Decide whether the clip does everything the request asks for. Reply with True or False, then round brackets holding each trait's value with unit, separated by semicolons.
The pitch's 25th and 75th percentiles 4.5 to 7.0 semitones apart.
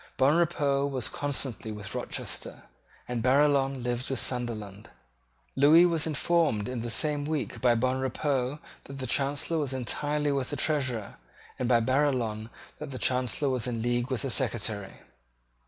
False (3.2 semitones)